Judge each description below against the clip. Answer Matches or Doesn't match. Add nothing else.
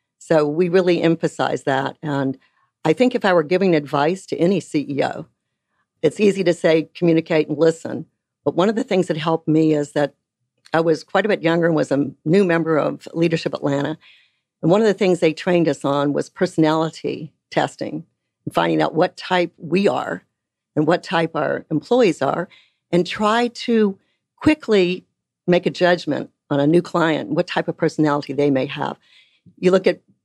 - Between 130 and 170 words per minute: Doesn't match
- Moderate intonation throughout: Matches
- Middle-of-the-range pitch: Matches